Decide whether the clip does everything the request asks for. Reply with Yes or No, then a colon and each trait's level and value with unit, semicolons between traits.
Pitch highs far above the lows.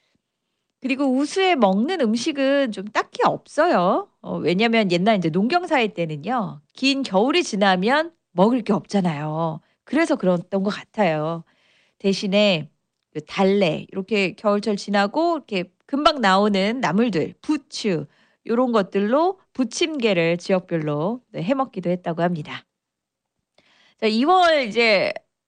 Yes: wide, 6.3 semitones